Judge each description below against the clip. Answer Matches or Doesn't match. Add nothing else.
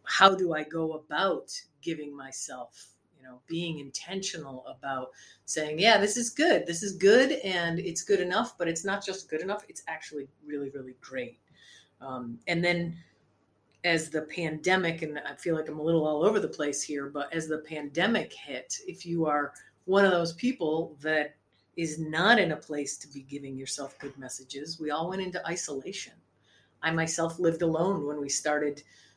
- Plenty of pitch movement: Doesn't match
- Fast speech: Doesn't match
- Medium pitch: Matches